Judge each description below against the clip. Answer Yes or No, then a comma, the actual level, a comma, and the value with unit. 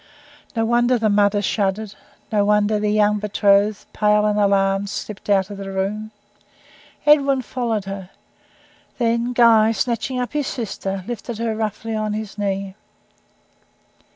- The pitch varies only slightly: Yes, narrow, 2.3 semitones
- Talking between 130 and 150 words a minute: Yes, average, 140 wpm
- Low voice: No, high, 210 Hz